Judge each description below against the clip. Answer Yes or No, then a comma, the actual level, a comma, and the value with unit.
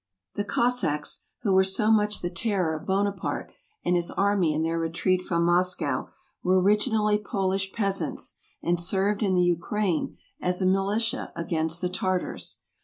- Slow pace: No, average, 155 wpm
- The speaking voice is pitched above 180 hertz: Yes, high, 190 Hz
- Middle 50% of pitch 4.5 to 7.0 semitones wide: No, average, 2.8 semitones